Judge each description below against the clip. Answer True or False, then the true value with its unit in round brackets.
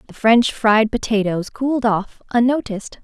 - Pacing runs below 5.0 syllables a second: True (4.7 syllables/s)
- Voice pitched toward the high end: True (225 Hz)